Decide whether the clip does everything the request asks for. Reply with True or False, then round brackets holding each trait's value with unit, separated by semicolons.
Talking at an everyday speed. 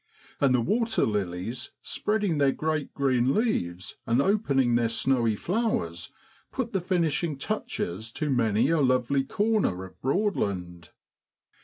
False (125 wpm)